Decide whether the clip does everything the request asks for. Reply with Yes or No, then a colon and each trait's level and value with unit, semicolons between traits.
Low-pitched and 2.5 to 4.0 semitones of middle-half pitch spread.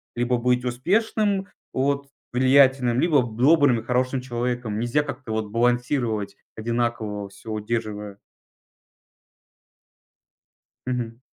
Yes: low, 120 Hz; average, 2.8 semitones